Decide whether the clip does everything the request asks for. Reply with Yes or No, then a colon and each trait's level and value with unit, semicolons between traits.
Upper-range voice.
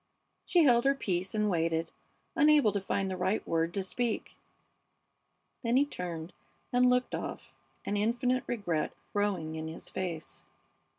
Yes: high, 205 Hz